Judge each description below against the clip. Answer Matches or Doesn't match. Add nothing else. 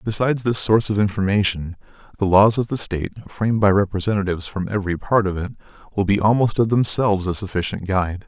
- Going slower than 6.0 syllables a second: Doesn't match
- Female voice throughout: Doesn't match